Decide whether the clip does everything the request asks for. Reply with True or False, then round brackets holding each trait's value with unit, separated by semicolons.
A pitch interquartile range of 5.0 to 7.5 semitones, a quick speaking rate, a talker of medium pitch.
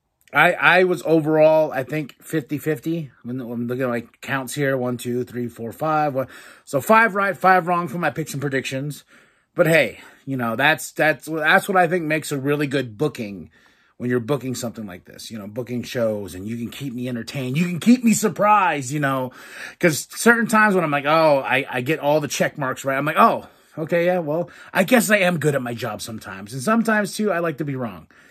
True (5.3 semitones; 225 wpm; 145 Hz)